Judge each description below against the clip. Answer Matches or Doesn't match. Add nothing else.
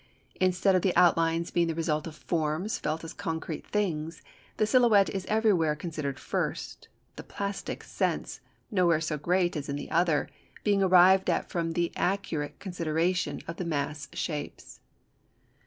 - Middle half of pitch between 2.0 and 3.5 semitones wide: Matches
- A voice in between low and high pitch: Matches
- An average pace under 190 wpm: Matches